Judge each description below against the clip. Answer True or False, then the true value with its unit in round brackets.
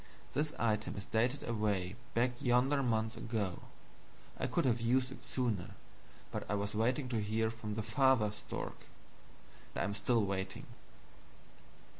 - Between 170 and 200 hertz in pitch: False (110 Hz)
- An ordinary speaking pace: True (145 wpm)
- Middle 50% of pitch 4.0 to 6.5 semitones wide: False (2.9 semitones)